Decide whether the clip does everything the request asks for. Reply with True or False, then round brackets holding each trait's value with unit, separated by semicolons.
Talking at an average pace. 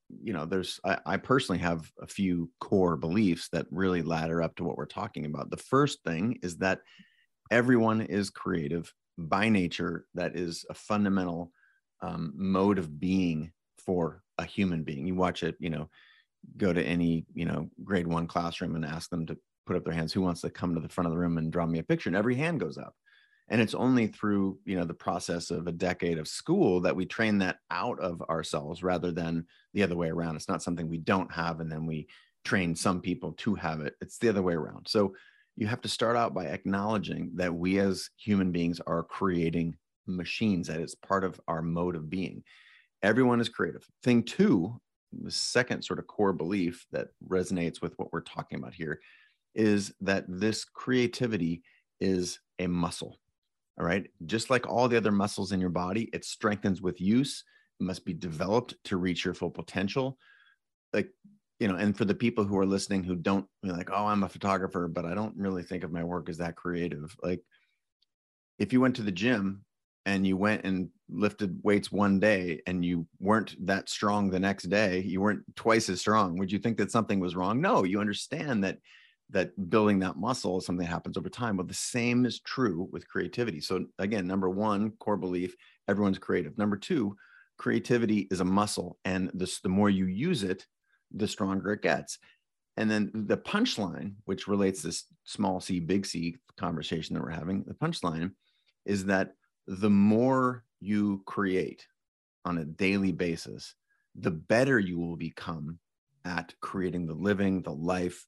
True (195 wpm)